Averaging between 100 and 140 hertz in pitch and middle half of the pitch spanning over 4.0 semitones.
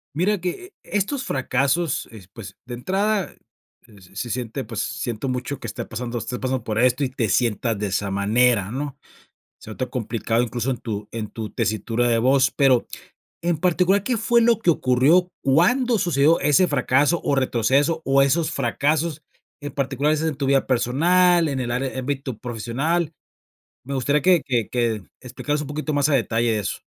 Yes: low, 135 Hz; average, 4.9 semitones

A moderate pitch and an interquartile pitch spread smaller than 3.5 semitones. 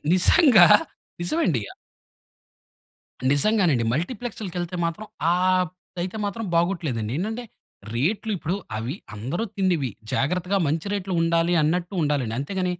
No: medium, 175 Hz; average, 4.6 semitones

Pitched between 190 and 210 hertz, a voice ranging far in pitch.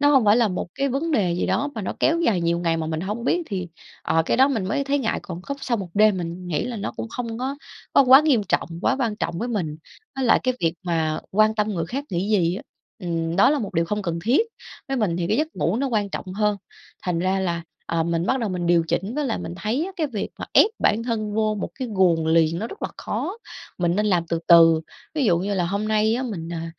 Yes: high, 205 Hz; wide, 6.0 semitones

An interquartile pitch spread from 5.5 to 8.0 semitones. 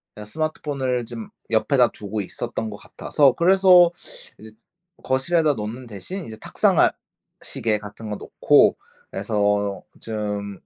No: average, 5.1 semitones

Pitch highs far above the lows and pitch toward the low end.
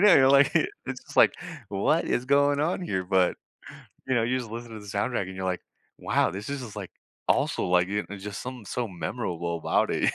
Yes: wide, 5.8 semitones; low, 110 Hz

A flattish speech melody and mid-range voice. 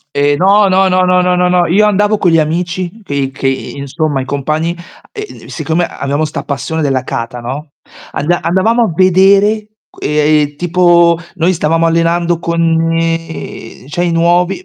No: average, 3.2 semitones; medium, 170 Hz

